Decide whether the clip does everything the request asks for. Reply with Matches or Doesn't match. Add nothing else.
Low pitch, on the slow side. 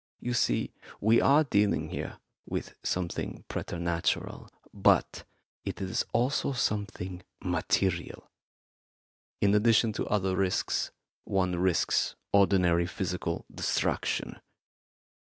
Matches